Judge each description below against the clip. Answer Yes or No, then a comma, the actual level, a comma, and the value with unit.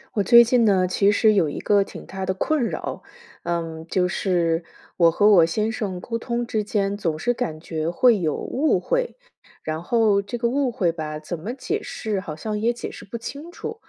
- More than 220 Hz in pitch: No, high, 200 Hz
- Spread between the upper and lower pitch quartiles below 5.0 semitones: No, wide, 5.6 semitones